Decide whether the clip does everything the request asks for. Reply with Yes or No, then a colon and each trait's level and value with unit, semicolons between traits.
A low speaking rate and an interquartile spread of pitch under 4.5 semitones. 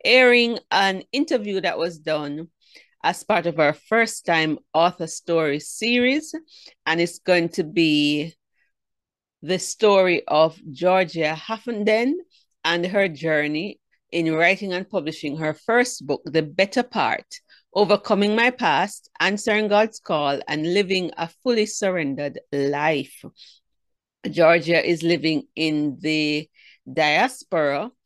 No: slow, 120 wpm; average, 5.3 semitones